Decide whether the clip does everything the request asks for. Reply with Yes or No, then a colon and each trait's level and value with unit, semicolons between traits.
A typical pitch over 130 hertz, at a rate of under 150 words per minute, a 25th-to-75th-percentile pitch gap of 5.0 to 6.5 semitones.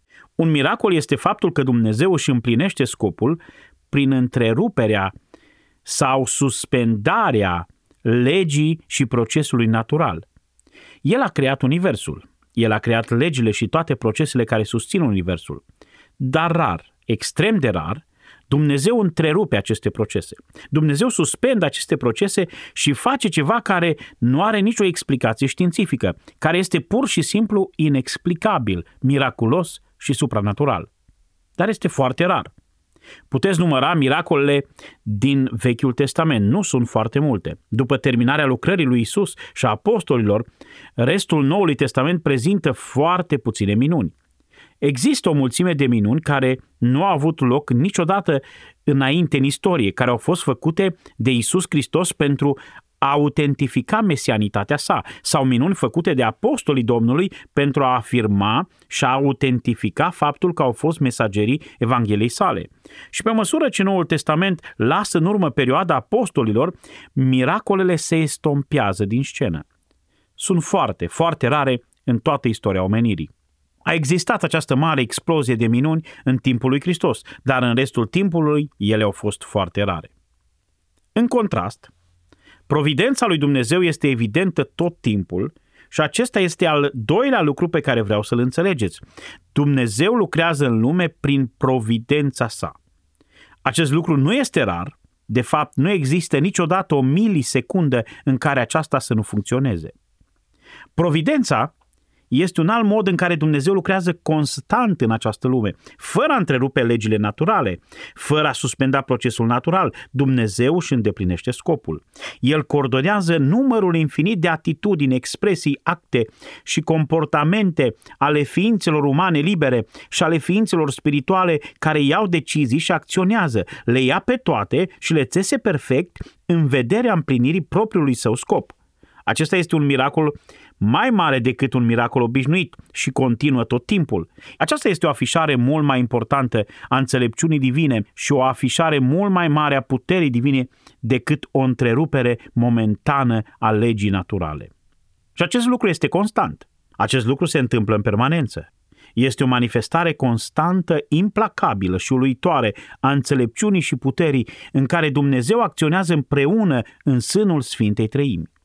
Yes: medium, 140 Hz; average, 135 wpm; wide, 5.6 semitones